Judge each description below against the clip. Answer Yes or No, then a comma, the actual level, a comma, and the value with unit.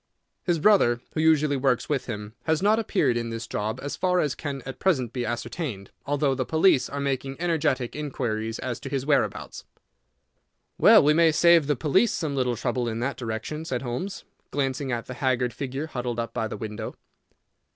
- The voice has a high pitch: No, low, 135 Hz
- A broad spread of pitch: No, average, 4.2 semitones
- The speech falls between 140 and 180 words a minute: No, average, 190 wpm